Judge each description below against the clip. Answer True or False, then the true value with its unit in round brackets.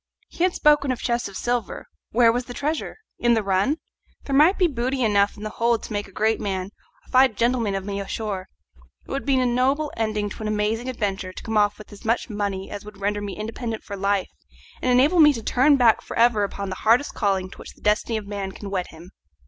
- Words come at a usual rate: False (245 wpm)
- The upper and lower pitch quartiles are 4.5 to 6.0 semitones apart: False (3.6 semitones)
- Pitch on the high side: True (220 Hz)